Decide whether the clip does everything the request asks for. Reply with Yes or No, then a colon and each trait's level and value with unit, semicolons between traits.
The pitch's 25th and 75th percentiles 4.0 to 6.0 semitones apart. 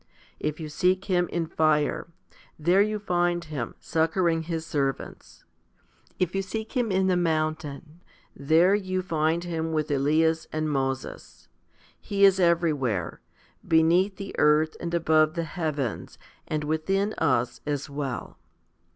No: average, 2.9 semitones